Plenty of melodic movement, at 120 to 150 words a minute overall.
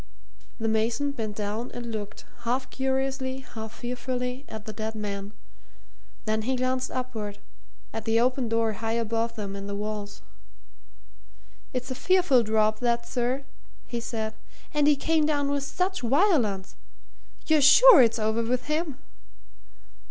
No: average, 3.5 semitones; average, 145 wpm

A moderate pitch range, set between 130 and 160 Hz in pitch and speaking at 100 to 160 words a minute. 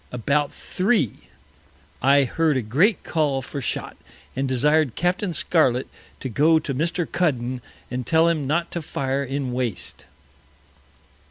Yes: average, 4.0 semitones; medium, 140 Hz; average, 140 wpm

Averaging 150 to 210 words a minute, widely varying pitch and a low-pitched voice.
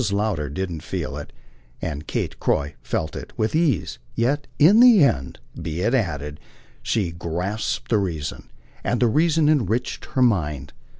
Yes: average, 155 wpm; wide, 8.7 semitones; low, 100 Hz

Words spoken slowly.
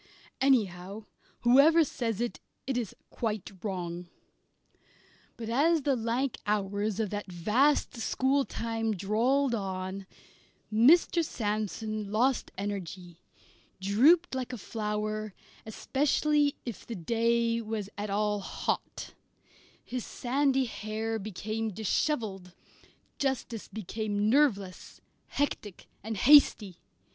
Yes: slow, 100 wpm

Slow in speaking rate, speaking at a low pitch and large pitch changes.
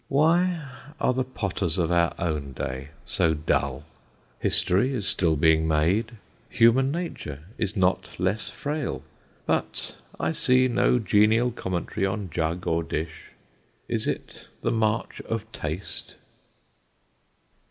Yes: slow, 125 wpm; very low, 95 Hz; wide, 7.2 semitones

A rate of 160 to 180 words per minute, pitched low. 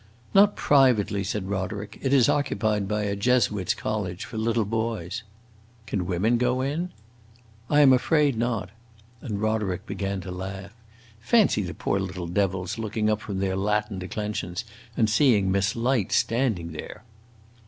No: average, 150 wpm; low, 105 Hz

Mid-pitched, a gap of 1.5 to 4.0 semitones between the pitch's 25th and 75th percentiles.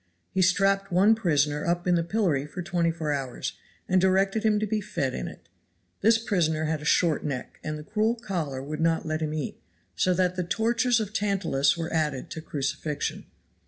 No: medium, 170 Hz; average, 4.4 semitones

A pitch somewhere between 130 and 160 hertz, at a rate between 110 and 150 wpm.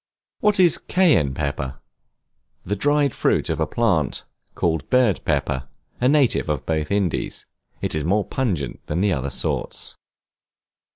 No: very low, 90 Hz; average, 140 wpm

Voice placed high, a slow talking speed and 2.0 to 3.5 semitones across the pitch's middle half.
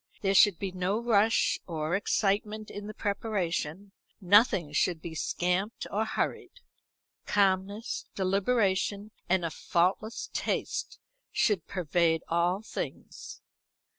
Yes: high, 195 Hz; slow, 110 wpm; average, 2.9 semitones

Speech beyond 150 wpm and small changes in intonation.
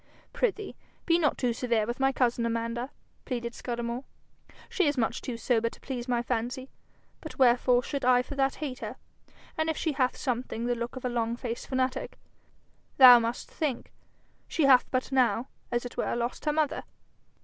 Yes: average, 180 wpm; narrow, 2.2 semitones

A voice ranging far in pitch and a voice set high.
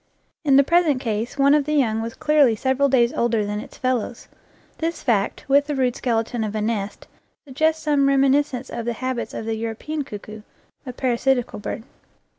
No: average, 3.8 semitones; very high, 255 Hz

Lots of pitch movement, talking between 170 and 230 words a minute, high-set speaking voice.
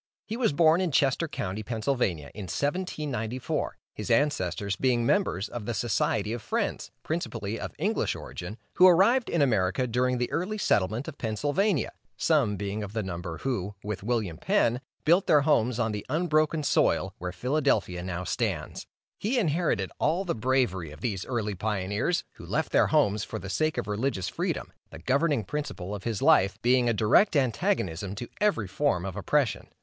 No: wide, 7.1 semitones; average, 175 wpm; low, 120 Hz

